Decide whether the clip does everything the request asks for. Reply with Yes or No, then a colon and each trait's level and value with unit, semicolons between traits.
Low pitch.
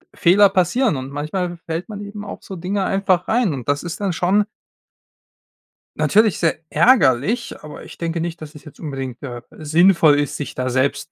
No: medium, 170 Hz